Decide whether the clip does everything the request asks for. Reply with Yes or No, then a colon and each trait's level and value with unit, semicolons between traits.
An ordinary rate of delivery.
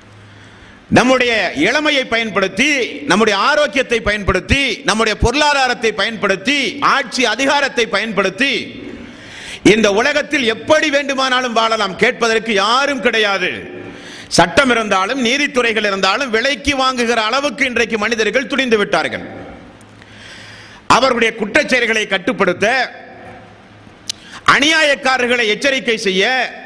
Yes: average, 85 wpm